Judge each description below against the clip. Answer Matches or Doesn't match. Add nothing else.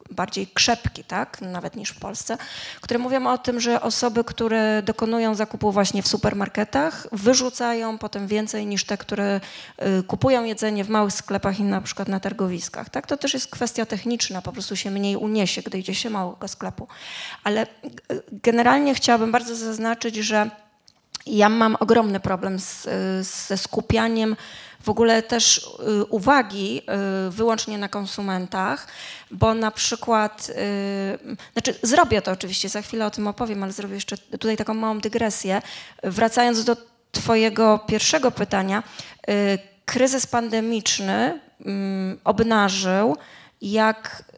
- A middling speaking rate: Matches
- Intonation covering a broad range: Doesn't match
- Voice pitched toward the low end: Doesn't match